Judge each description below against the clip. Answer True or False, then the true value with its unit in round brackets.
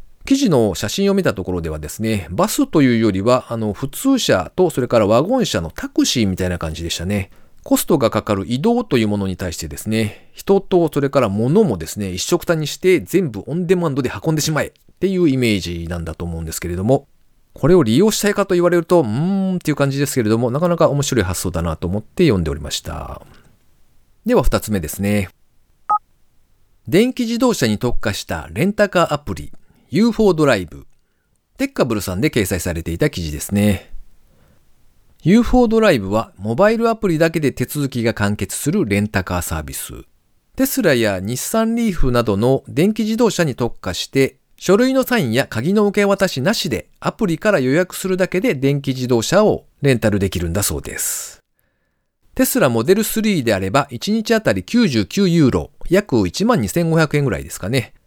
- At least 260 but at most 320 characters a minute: False (370 characters per minute)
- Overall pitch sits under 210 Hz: True (135 Hz)